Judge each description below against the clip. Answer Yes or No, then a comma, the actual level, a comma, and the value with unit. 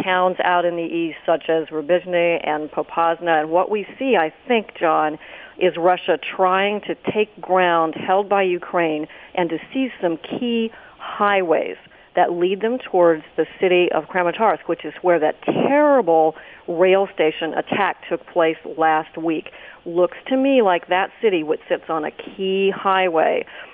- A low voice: No, medium, 180 Hz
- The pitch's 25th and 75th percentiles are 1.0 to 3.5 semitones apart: Yes, average, 3.2 semitones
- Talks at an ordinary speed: Yes, average, 160 wpm